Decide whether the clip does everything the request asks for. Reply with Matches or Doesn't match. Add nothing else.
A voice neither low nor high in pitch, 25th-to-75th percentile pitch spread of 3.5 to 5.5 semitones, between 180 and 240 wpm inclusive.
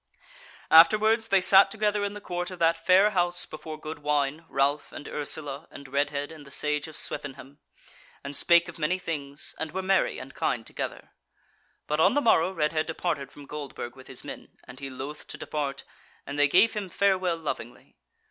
Matches